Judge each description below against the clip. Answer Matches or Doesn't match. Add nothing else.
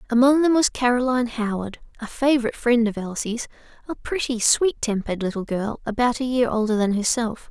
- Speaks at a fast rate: Doesn't match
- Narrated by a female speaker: Matches